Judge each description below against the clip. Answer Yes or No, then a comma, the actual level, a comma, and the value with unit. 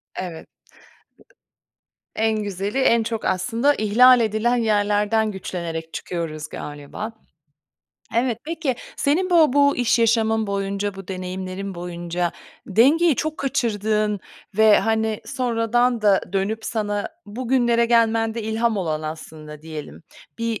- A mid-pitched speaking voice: No, high, 220 Hz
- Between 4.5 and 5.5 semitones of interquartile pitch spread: No, average, 3.5 semitones